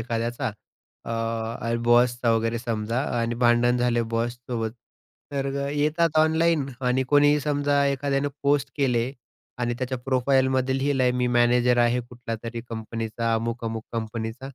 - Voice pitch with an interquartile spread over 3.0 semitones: No, average, 2.7 semitones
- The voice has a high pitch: No, low, 120 Hz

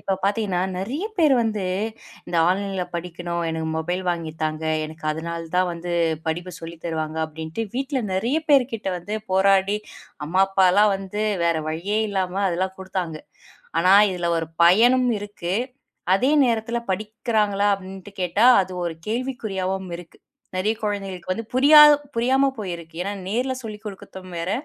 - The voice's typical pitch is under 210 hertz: Yes, high, 190 Hz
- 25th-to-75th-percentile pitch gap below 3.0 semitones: No, average, 3.8 semitones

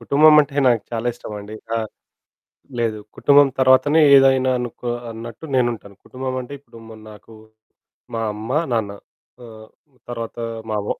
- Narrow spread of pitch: No, average, 3.0 semitones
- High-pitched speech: No, low, 120 Hz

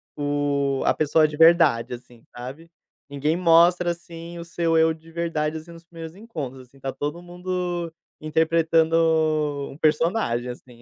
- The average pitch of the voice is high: No, medium, 160 Hz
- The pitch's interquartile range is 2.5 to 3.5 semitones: Yes, average, 2.9 semitones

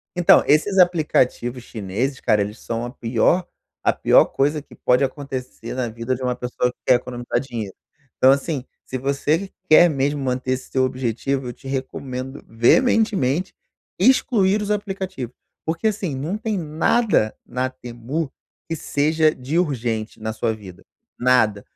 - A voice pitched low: Yes, low, 130 Hz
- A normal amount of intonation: Yes, average, 4.8 semitones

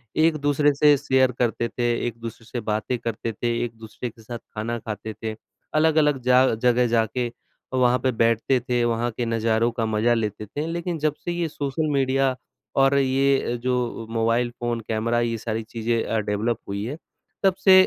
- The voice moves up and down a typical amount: Yes, average, 3.1 semitones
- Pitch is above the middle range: No, low, 120 Hz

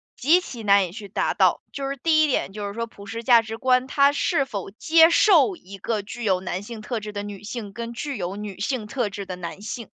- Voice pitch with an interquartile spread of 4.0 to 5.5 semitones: Yes, average, 4.7 semitones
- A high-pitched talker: Yes, high, 225 Hz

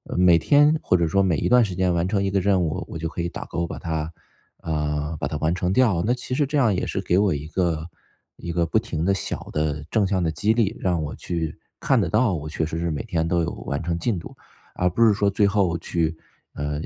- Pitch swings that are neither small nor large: Yes, average, 3.7 semitones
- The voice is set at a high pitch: No, very low, 85 Hz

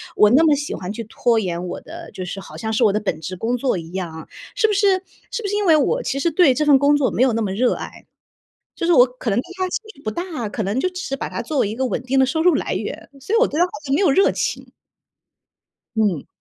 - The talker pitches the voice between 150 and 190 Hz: No, very high, 260 Hz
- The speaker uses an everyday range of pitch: No, wide, 7.8 semitones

